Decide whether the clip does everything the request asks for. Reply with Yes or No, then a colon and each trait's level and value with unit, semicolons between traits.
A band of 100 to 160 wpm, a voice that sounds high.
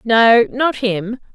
Yes: slow, 135 wpm; high, 235 Hz